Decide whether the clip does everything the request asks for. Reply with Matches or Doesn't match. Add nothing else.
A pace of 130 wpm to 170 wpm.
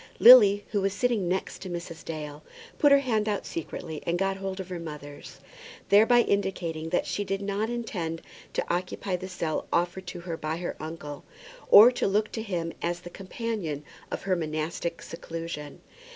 Doesn't match